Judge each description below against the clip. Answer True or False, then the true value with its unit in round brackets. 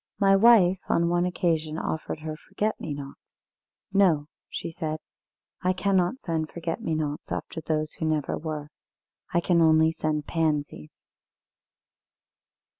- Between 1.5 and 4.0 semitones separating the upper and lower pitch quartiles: True (2.7 semitones)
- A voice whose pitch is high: False (160 Hz)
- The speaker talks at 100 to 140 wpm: True (135 wpm)